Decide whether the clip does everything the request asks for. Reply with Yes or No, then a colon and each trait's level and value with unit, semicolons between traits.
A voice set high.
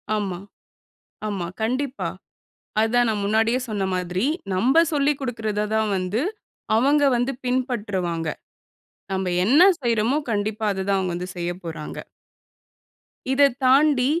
Yes: high, 220 Hz